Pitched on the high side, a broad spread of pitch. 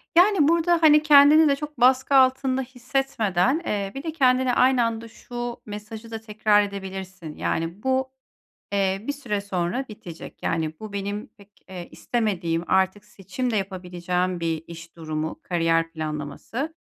Yes: high, 210 Hz; wide, 6.3 semitones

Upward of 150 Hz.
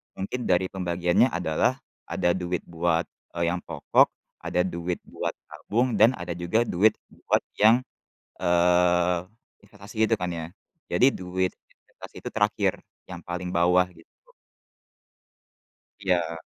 No: very low, 90 Hz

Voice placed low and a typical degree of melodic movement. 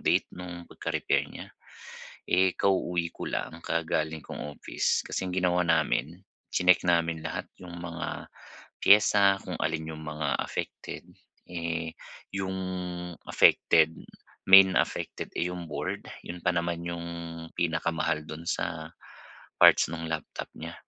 No: very low, 85 Hz; narrow, 1.9 semitones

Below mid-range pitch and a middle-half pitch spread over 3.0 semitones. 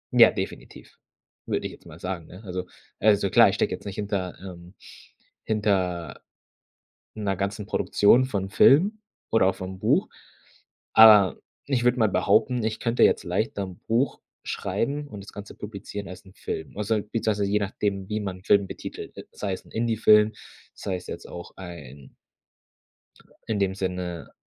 No: low, 100 Hz; average, 2.7 semitones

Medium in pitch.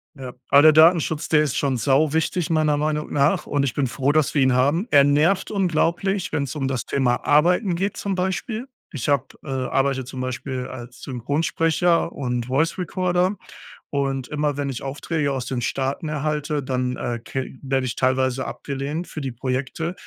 Yes: medium, 145 Hz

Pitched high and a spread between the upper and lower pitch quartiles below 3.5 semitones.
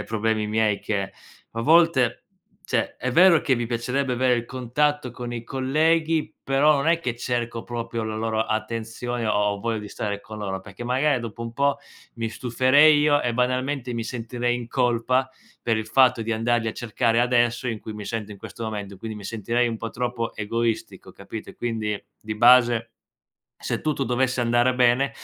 No: low, 120 Hz; narrow, 2.5 semitones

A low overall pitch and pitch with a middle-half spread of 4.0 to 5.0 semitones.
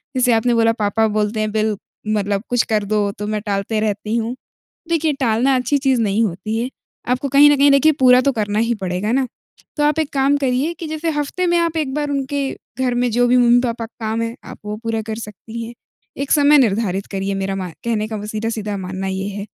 No: high, 230 Hz; average, 4.3 semitones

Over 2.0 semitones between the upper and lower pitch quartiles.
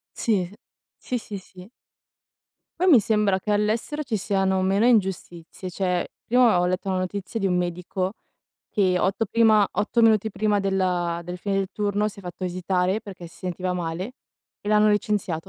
Yes: average, 2.7 semitones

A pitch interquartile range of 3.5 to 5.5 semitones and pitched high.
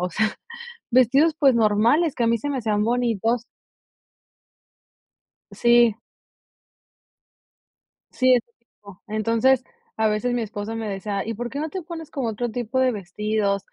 No: average, 3.1 semitones; high, 230 Hz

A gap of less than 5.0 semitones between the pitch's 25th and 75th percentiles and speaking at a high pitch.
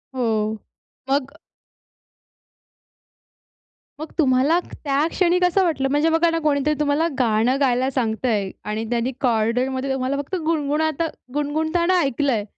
Yes: average, 4.1 semitones; very high, 275 Hz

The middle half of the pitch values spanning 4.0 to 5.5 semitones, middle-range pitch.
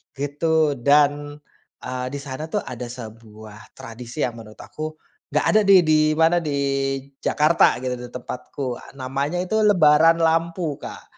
Yes: average, 4.3 semitones; medium, 145 Hz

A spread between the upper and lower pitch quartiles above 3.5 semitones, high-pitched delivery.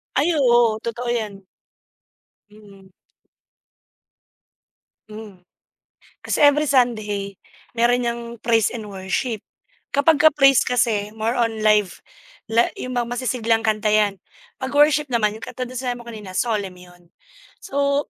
No: average, 3.2 semitones; high, 230 Hz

